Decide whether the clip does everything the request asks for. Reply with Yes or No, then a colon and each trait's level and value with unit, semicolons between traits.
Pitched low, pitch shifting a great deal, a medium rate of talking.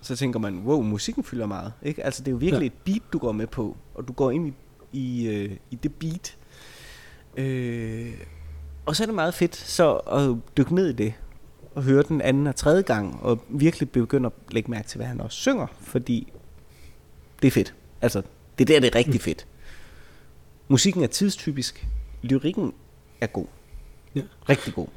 Yes: low, 125 Hz; wide, 7.2 semitones; average, 190 wpm